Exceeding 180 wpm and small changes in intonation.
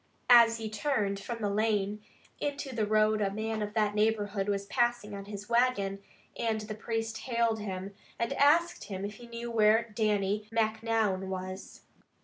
No: average, 160 wpm; narrow, 2.2 semitones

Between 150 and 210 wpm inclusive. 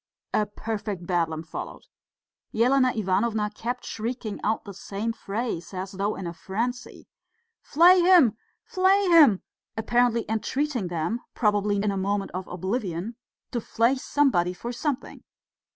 No: slow, 135 wpm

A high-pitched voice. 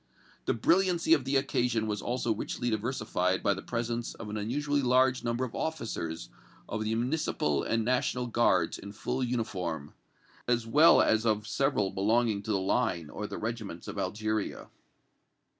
No: low, 115 Hz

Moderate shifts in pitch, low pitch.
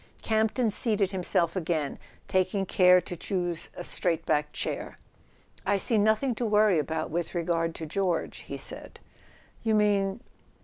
No: average, 3.9 semitones; medium, 185 Hz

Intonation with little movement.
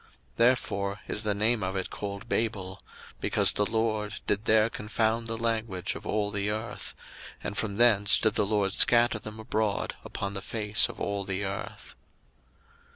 Yes: narrow, 1.8 semitones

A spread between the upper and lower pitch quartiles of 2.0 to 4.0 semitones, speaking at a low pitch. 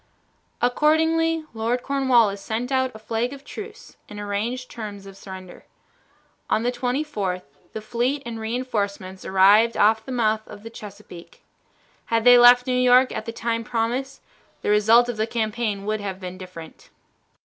No: average, 3.4 semitones; high, 230 Hz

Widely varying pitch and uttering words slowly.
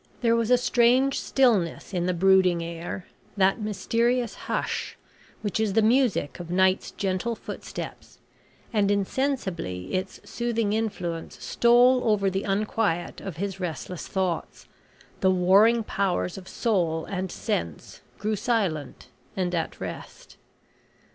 No: average, 4.2 semitones; slow, 130 wpm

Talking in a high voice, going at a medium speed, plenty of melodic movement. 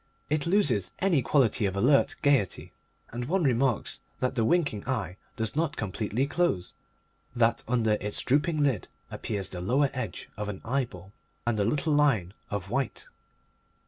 No: low, 120 Hz; average, 155 wpm; wide, 5.7 semitones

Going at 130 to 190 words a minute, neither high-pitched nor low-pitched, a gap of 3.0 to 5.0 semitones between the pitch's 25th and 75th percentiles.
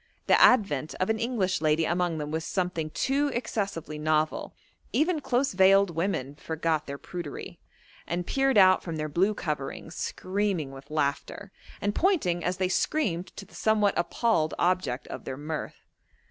Yes: average, 160 wpm; medium, 180 Hz; average, 4.7 semitones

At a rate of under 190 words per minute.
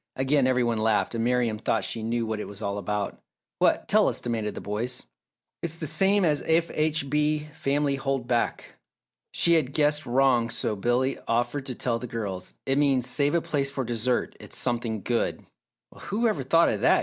No: average, 200 wpm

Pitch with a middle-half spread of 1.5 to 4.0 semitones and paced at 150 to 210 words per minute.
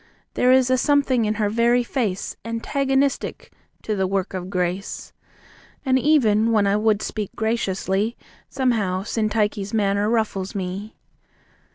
No: average, 3.6 semitones; slow, 135 wpm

